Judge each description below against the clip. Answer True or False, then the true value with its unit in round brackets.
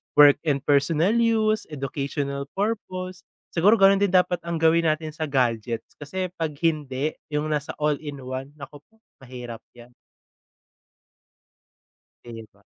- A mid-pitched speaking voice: True (150 Hz)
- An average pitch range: True (4.5 semitones)